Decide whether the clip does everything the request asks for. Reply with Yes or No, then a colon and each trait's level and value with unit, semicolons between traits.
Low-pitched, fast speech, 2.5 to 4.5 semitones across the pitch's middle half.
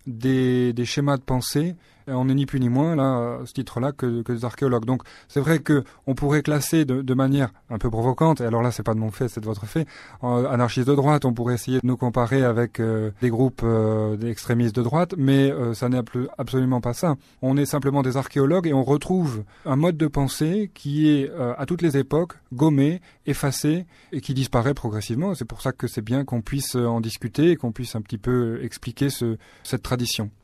Yes: low, 130 Hz; fast, 225 wpm; average, 2.9 semitones